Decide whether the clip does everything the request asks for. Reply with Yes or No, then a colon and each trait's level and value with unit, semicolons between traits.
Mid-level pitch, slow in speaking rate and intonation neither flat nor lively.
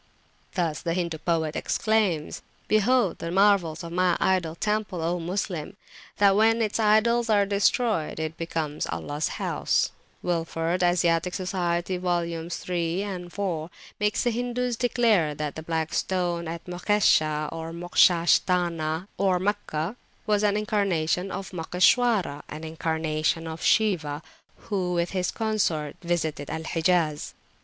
Yes: medium, 175 Hz; slow, 130 wpm; average, 3.8 semitones